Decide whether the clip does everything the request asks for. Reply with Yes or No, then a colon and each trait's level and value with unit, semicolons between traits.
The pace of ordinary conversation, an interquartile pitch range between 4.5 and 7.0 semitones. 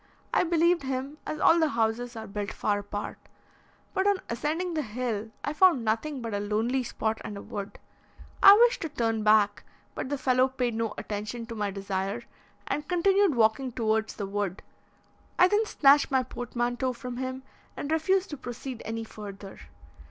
Yes: average, 175 wpm; wide, 5.4 semitones